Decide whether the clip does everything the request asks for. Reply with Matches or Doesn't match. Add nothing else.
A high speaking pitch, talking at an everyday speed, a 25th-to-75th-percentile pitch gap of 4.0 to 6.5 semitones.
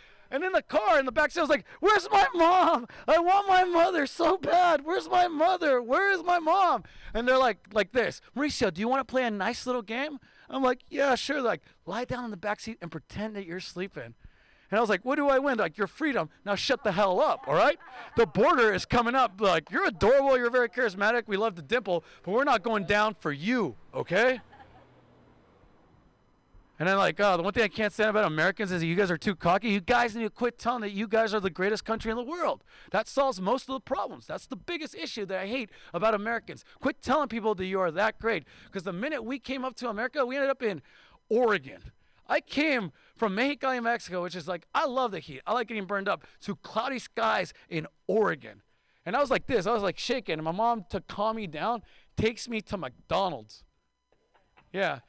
Doesn't match